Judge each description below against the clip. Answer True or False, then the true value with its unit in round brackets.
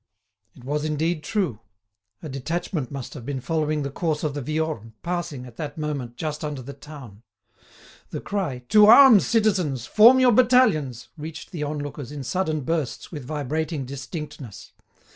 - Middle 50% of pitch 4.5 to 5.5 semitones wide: False (3.9 semitones)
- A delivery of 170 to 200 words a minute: False (160 wpm)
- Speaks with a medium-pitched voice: True (150 Hz)